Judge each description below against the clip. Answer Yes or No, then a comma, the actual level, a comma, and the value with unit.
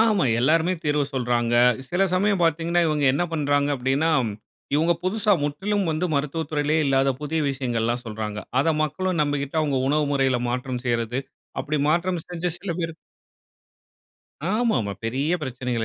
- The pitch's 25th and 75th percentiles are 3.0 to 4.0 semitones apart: No, average, 4.4 semitones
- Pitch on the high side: No, medium, 150 Hz